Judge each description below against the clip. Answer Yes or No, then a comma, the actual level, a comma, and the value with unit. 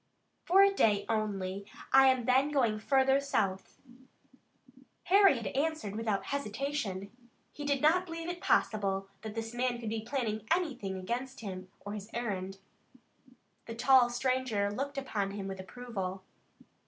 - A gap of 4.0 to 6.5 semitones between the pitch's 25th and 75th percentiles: Yes, average, 5.2 semitones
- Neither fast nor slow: Yes, average, 145 wpm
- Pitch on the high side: Yes, high, 230 Hz